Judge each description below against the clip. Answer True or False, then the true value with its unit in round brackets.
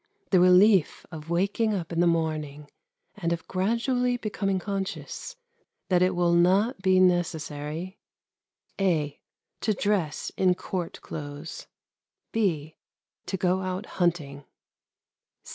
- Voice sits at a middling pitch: True (180 Hz)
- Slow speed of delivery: True (115 wpm)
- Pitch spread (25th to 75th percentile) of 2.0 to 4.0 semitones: True (3.3 semitones)